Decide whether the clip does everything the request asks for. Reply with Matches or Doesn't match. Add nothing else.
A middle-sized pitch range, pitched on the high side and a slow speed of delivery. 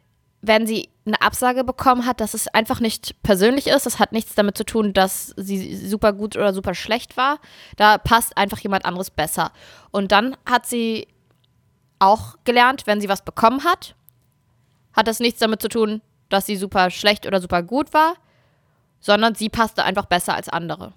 Doesn't match